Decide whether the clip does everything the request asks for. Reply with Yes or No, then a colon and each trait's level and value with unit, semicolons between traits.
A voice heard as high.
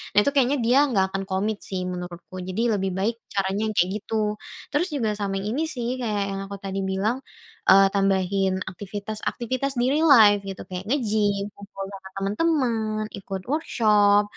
Yes: high, 205 Hz